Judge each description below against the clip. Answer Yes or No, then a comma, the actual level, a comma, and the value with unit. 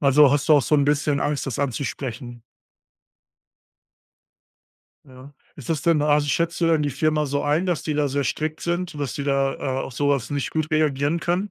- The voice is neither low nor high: Yes, medium, 145 Hz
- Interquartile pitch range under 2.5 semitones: Yes, narrow, 2.1 semitones